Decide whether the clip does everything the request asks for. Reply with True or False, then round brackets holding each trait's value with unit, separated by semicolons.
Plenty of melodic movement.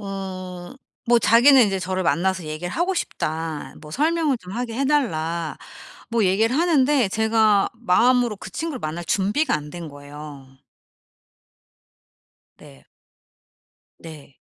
True (7.1 semitones)